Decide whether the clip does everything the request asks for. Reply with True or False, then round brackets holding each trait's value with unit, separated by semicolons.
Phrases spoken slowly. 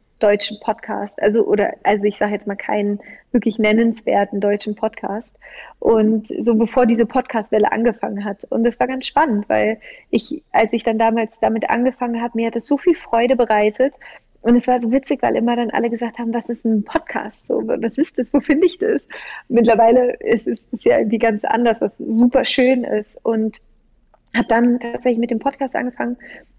False (190 wpm)